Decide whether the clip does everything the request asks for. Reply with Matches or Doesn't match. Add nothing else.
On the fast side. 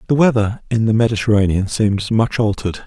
Doesn't match